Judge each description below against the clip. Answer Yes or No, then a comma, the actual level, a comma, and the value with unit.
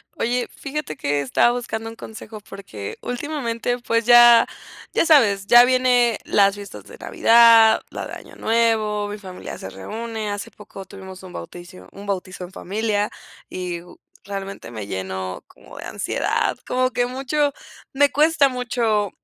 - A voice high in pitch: Yes, high, 220 Hz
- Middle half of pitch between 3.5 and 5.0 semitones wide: Yes, average, 4.1 semitones